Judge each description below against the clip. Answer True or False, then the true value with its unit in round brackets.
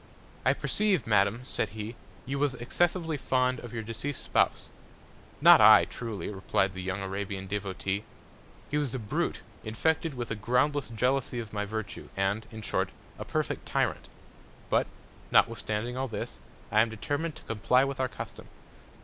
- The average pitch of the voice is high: False (115 Hz)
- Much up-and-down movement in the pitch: False (4.3 semitones)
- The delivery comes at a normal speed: True (160 wpm)